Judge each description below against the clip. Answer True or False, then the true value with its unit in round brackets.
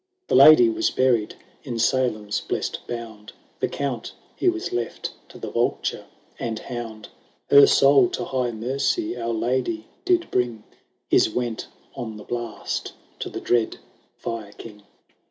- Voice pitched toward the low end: True (120 Hz)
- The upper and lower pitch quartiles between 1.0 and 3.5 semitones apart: True (2.8 semitones)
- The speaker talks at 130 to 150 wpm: True (145 wpm)